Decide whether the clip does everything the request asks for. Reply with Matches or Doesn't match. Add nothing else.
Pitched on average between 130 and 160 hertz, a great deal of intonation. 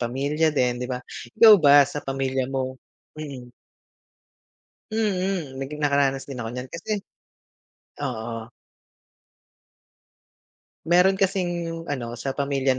Doesn't match